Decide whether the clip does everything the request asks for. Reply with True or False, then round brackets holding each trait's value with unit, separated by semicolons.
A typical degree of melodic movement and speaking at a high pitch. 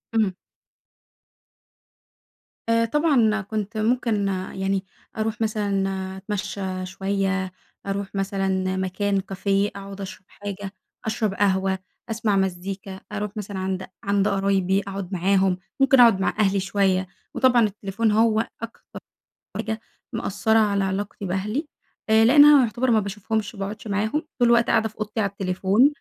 False (2.2 semitones; 200 Hz)